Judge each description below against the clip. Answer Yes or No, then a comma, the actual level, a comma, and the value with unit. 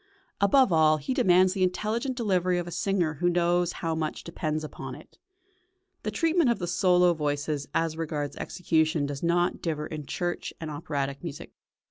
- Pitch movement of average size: Yes, average, 3.1 semitones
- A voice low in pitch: No, medium, 170 Hz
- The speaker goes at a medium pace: Yes, average, 170 wpm